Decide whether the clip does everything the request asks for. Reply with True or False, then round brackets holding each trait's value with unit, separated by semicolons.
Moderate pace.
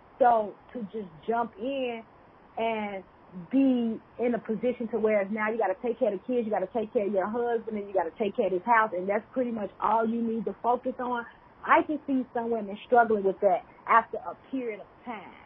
False (225 wpm)